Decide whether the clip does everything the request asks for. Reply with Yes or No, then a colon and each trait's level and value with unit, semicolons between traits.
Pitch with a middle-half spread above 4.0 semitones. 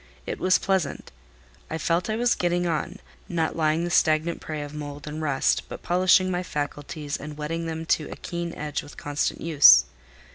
No: average, 2.7 semitones